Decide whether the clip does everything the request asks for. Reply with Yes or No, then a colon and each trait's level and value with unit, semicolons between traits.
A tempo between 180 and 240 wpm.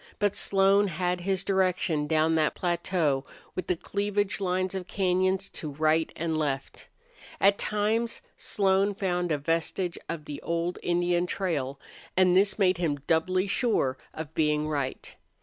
No: average, 150 wpm